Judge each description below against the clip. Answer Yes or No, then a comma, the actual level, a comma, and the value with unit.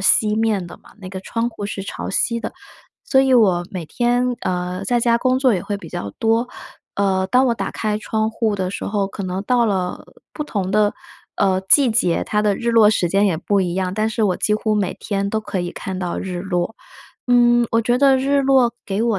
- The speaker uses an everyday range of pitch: Yes, average, 3.8 semitones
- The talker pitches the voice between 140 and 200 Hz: No, high, 210 Hz